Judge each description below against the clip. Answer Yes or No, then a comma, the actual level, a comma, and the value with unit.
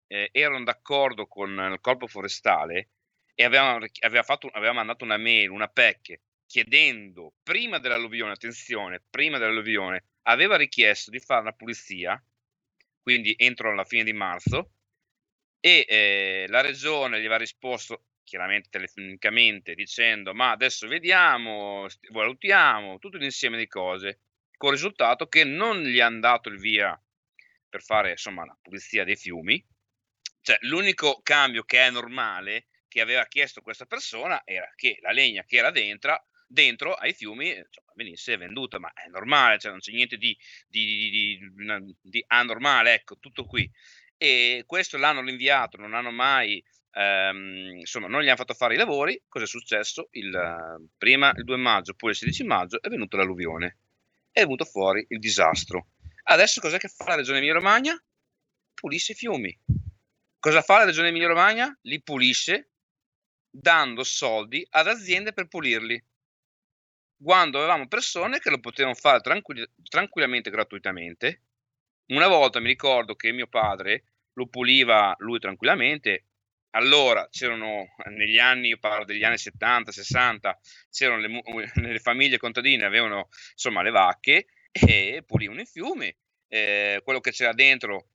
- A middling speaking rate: Yes, average, 150 wpm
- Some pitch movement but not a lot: Yes, average, 4.4 semitones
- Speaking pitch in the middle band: No, low, 115 Hz